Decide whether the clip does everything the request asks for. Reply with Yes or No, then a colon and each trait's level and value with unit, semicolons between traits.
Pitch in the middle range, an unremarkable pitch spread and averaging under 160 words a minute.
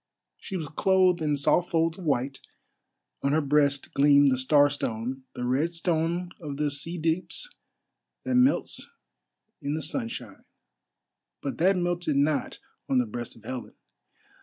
Yes: medium, 150 Hz; average, 4.0 semitones; average, 145 wpm